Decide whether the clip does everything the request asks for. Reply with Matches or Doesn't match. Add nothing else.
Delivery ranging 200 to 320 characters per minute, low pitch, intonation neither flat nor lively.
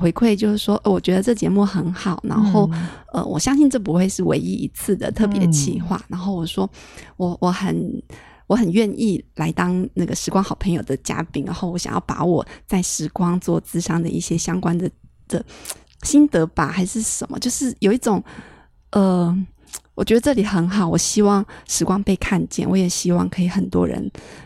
Doesn't match